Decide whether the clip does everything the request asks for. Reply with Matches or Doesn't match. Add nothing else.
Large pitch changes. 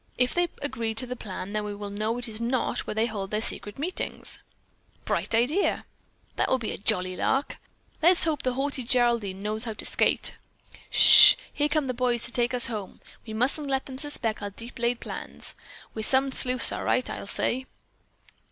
Doesn't match